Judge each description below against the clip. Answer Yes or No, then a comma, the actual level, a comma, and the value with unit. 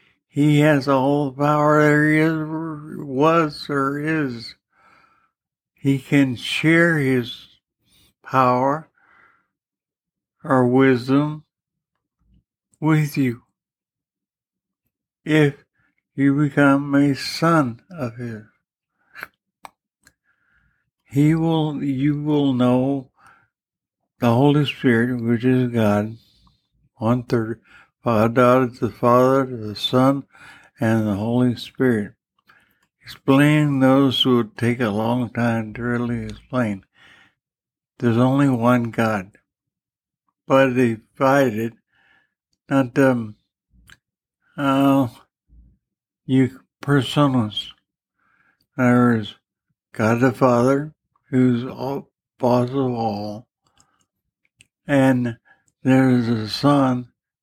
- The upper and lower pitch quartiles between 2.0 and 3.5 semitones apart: Yes, average, 2.9 semitones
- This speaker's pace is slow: Yes, slow, 90 wpm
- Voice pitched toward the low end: Yes, low, 130 Hz